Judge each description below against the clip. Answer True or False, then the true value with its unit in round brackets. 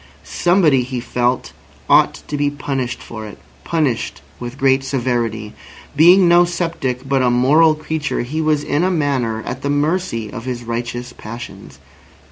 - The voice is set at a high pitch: False (135 Hz)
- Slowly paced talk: False (150 wpm)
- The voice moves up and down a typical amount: True (4.1 semitones)